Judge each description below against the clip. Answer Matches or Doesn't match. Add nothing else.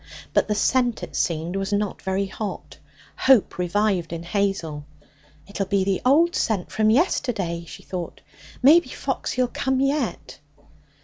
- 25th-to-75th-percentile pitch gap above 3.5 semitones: Matches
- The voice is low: Doesn't match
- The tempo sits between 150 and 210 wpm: Doesn't match